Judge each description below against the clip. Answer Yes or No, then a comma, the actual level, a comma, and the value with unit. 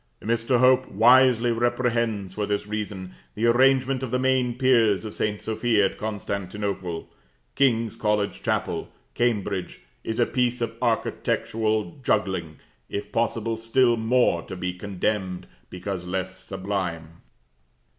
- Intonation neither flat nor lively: Yes, average, 3.7 semitones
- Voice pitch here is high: No, low, 110 Hz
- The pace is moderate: No, slow, 125 wpm